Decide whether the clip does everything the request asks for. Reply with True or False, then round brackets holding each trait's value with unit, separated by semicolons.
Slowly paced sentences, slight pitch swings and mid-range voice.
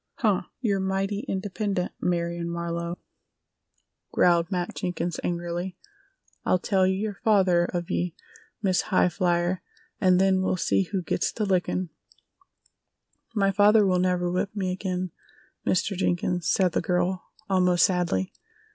True (130 wpm; 1.7 semitones; 180 Hz)